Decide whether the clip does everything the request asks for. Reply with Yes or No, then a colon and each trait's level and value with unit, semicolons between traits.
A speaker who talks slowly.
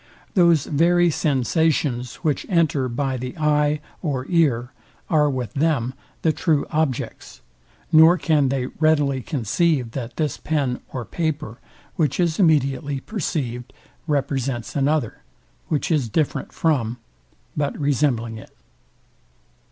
Yes: slow, 120 wpm